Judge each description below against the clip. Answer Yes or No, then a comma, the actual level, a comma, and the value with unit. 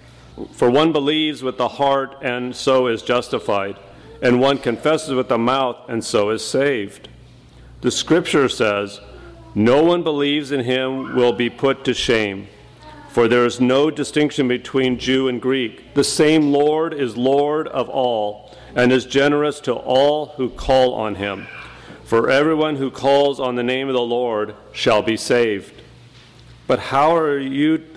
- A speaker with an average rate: Yes, average, 160 wpm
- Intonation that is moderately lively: Yes, average, 3.2 semitones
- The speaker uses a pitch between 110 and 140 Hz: Yes, low, 130 Hz